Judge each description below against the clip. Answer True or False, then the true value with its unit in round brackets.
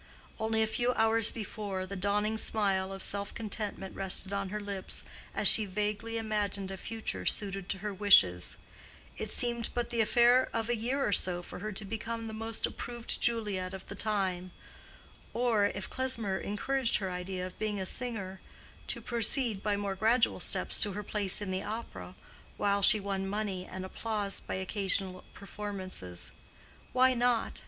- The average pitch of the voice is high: True (205 Hz)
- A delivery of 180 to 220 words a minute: False (170 wpm)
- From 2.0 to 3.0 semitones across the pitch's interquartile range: True (2.7 semitones)